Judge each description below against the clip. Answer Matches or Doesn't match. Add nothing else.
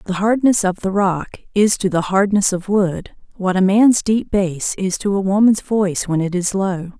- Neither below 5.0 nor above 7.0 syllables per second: Doesn't match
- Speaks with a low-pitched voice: Doesn't match